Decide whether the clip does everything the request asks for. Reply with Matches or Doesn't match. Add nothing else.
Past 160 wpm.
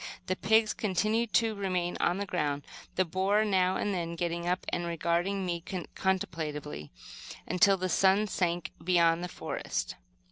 Doesn't match